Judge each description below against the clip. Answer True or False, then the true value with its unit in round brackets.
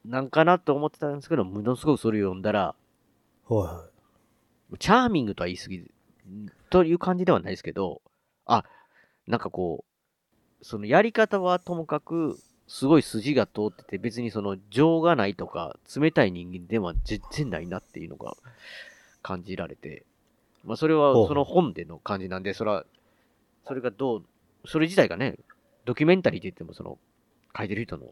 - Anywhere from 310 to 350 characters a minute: True (325 characters per minute)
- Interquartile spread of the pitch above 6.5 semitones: True (8.0 semitones)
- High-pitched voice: False (125 Hz)